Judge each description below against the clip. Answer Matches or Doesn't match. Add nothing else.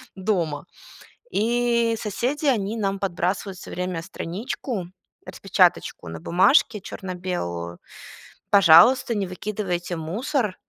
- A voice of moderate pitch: Doesn't match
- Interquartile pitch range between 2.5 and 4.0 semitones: Doesn't match